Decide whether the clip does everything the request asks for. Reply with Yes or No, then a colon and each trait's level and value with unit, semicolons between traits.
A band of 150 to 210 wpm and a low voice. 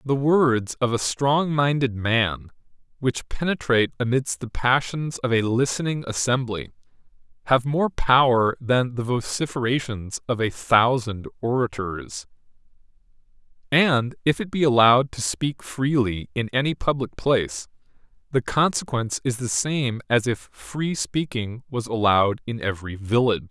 No: slow, 135 wpm; low, 125 Hz